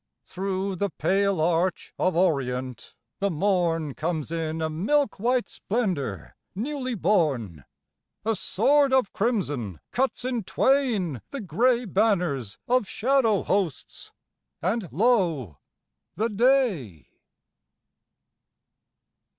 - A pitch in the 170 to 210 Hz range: Yes, high, 190 Hz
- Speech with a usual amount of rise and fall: No, wide, 6.8 semitones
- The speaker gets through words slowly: Yes, slow, 100 wpm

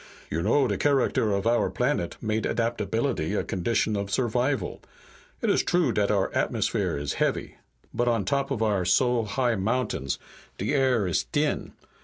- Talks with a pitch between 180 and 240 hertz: No, low, 110 Hz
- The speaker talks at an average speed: Yes, average, 165 wpm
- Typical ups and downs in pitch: Yes, average, 4.2 semitones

